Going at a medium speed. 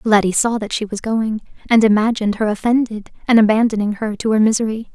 Yes: average, 195 wpm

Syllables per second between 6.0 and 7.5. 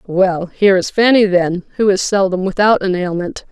No: 4.9 syllables/s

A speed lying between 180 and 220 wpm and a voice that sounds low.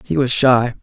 Yes: fast, 215 wpm; low, 125 Hz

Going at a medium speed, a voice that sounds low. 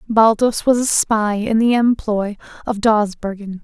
No: average, 150 wpm; high, 215 Hz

